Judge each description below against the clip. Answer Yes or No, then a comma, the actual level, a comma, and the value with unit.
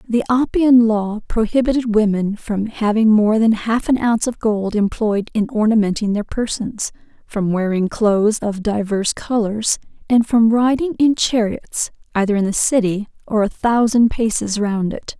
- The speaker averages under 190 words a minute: Yes, average, 160 wpm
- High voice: Yes, high, 220 Hz